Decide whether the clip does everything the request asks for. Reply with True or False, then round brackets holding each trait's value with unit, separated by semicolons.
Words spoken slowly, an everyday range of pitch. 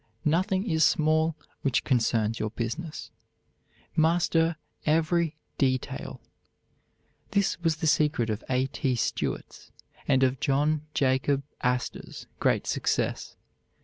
True (110 wpm; 3.9 semitones)